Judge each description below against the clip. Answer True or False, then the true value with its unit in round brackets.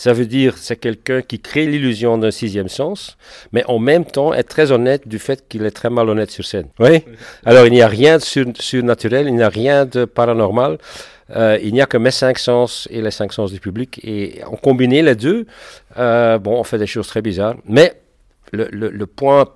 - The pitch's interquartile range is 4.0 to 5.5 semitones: False (3.2 semitones)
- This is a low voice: True (120 Hz)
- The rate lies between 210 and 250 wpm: True (220 wpm)